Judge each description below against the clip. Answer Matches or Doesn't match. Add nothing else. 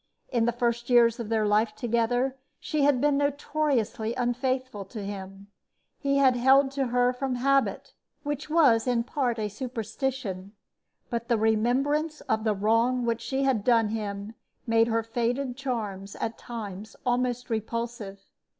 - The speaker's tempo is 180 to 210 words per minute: Doesn't match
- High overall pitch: Matches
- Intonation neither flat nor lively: Matches